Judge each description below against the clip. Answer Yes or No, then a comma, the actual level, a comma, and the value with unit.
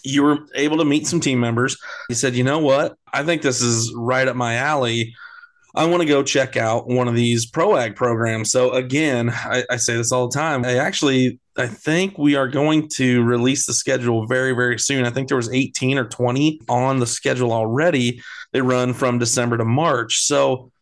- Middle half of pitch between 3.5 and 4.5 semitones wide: No, average, 2.8 semitones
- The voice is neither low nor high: No, low, 130 Hz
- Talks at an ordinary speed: No, fast, 215 wpm